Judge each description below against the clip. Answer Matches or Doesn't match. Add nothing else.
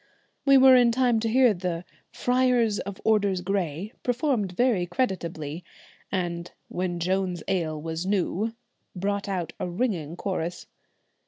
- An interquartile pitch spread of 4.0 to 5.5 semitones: Matches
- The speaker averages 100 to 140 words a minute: Matches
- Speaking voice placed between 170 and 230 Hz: Matches